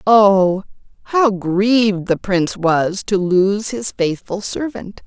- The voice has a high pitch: Yes, high, 200 Hz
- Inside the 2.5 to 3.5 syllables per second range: Yes, 3.4 syllables/s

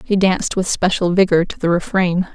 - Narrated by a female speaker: Yes, female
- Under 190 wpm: No, fast, 205 wpm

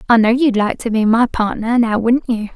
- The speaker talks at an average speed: No, fast, 260 wpm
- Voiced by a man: No, female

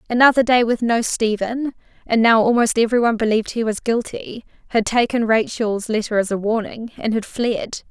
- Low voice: No, high, 225 Hz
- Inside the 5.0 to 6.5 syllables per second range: Yes, 5.4 syllables/s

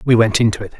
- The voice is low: Yes, low, 110 Hz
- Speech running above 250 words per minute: Yes, fast, 305 wpm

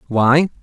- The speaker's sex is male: Yes, male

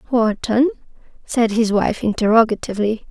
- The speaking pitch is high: Yes, high, 225 Hz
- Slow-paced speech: Yes, slow, 95 wpm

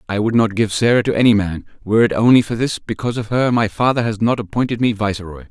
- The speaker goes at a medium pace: No, fast, 250 wpm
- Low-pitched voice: Yes, low, 110 Hz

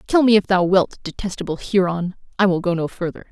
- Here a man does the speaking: No, female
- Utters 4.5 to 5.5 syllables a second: No, 5.9 syllables/s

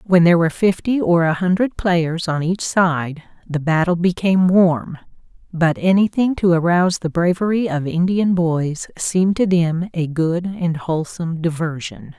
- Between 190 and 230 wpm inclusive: No, average, 160 wpm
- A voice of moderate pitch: Yes, medium, 175 Hz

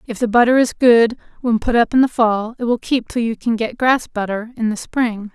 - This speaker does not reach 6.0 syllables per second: Yes, 5.1 syllables/s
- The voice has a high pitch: Yes, high, 230 Hz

